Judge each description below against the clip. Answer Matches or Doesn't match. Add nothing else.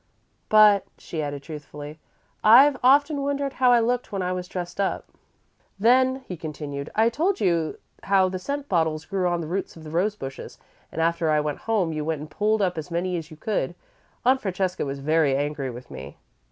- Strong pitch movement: Matches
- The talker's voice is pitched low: Doesn't match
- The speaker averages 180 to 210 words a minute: Matches